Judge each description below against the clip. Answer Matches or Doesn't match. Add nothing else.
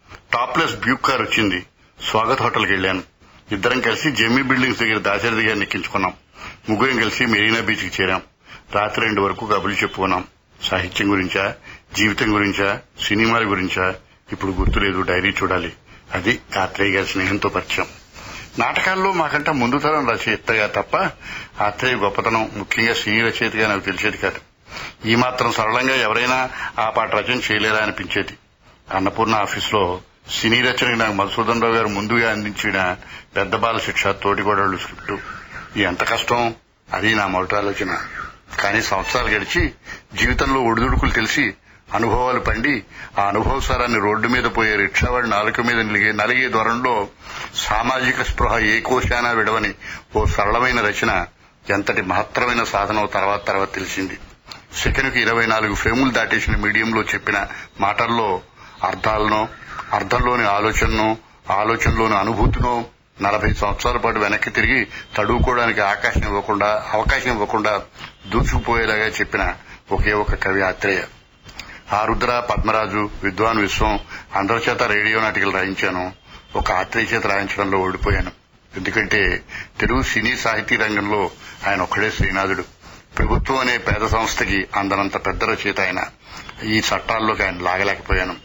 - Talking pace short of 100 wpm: Doesn't match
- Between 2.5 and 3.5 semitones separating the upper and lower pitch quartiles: Matches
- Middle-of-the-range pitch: Doesn't match